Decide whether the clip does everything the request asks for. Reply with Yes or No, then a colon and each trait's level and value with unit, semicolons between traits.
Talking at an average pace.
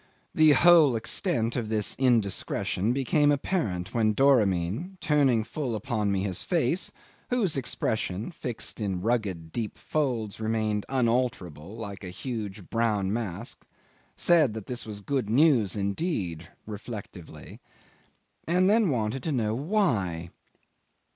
No: slow, 125 wpm